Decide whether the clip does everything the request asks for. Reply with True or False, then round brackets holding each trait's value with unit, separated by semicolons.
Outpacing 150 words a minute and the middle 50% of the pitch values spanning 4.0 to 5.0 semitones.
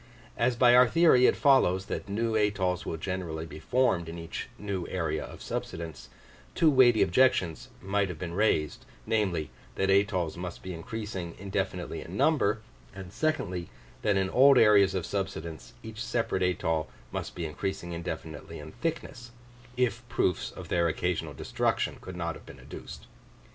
True (160 wpm; 4.7 semitones)